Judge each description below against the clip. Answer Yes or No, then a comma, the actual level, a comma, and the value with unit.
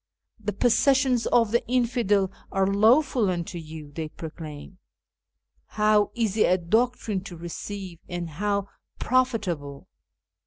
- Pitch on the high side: Yes, high, 200 Hz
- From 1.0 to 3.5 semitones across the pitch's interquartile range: No, average, 5.2 semitones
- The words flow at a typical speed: No, slow, 115 wpm